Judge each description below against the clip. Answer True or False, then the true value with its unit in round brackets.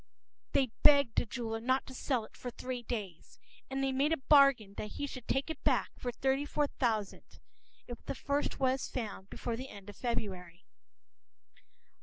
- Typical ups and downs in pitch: True (3.6 semitones)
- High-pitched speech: True (250 Hz)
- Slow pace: False (185 wpm)